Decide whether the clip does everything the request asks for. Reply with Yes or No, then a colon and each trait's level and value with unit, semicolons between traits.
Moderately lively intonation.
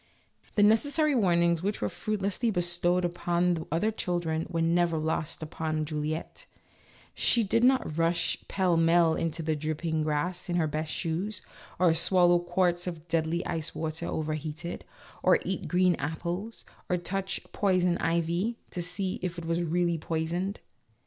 No: narrow, 2.2 semitones